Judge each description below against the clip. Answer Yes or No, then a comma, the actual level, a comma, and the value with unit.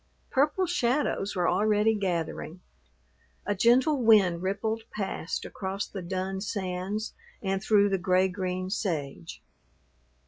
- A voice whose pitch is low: No, high, 195 Hz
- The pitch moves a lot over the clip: No, average, 2.8 semitones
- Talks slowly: Yes, slow, 115 wpm